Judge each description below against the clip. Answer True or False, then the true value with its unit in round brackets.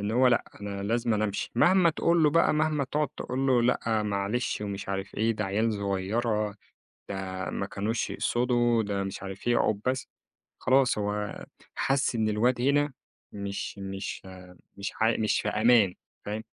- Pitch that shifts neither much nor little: True (3.7 semitones)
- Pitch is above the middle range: False (110 Hz)